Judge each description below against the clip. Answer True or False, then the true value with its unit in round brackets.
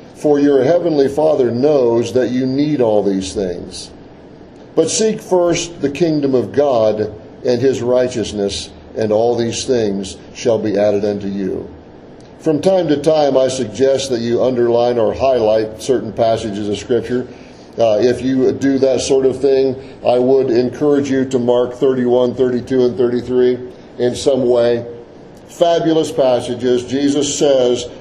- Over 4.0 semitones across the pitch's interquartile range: False (2.8 semitones)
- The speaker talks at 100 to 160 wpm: True (150 wpm)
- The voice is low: True (125 Hz)